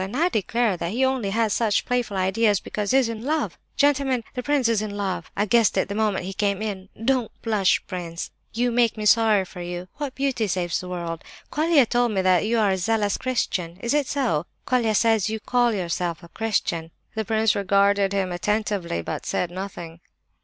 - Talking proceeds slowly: No, fast, 205 wpm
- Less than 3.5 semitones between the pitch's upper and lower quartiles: No, average, 4.0 semitones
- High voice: Yes, high, 210 Hz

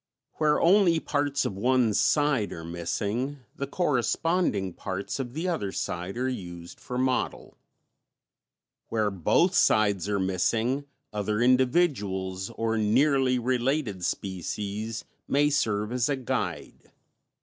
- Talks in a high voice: No, low, 120 Hz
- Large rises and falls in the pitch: Yes, wide, 5.7 semitones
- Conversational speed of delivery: No, slow, 120 wpm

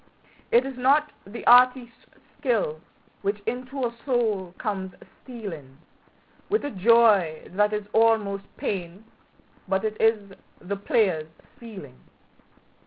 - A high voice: Yes, high, 215 Hz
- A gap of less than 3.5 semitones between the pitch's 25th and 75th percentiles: No, average, 4.0 semitones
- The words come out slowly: Yes, slow, 115 wpm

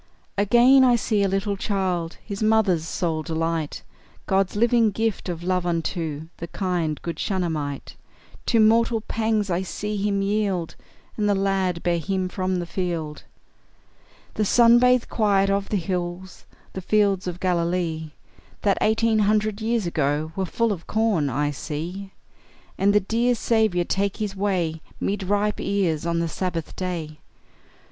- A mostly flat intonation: No, average, 3.8 semitones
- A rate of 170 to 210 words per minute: No, average, 155 wpm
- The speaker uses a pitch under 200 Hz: Yes, high, 190 Hz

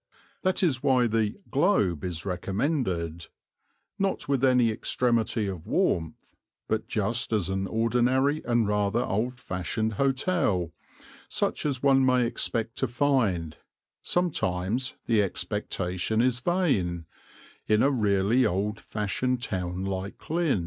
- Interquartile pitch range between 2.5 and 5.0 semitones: No, wide, 5.4 semitones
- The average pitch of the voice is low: Yes, low, 115 Hz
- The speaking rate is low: Yes, slow, 125 wpm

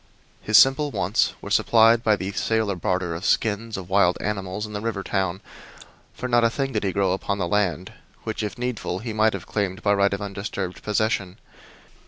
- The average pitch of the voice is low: Yes, low, 100 Hz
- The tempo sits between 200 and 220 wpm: Yes, fast, 205 wpm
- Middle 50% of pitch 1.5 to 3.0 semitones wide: Yes, narrow, 2.6 semitones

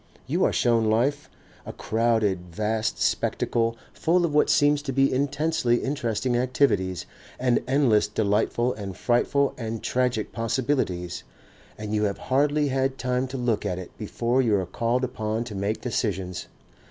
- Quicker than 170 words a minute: No, average, 155 wpm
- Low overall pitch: Yes, low, 120 Hz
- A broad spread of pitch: No, average, 3.8 semitones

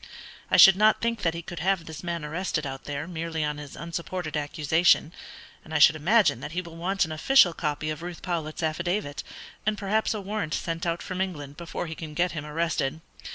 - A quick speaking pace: Yes, fast, 210 wpm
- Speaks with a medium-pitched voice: Yes, medium, 165 Hz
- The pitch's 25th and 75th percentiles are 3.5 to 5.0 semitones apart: No, average, 3.0 semitones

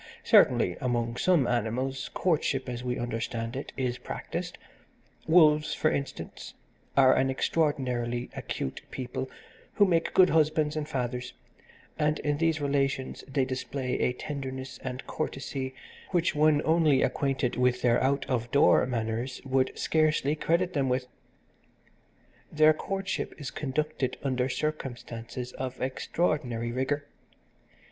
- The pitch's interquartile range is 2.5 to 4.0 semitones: Yes, average, 3.3 semitones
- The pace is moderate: No, slow, 125 wpm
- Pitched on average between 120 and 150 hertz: Yes, low, 135 Hz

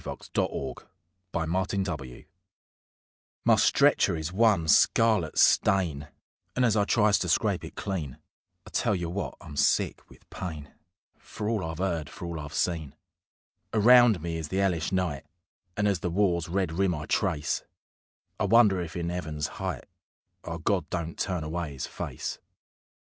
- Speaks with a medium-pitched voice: No, very low, 85 Hz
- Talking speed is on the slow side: No, average, 155 wpm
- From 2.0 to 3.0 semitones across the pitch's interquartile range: No, average, 3.5 semitones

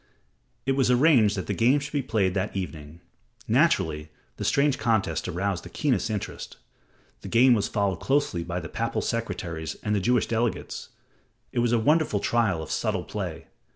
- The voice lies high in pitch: No, low, 110 Hz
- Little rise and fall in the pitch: No, average, 5.2 semitones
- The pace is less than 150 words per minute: No, average, 175 wpm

